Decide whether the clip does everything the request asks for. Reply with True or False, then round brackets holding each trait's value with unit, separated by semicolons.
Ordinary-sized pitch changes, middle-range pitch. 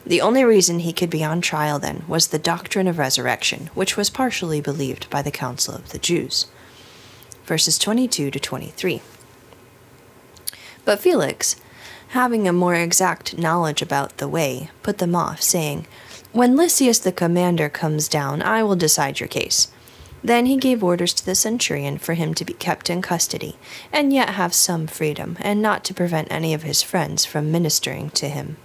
True (4.4 semitones; 170 Hz)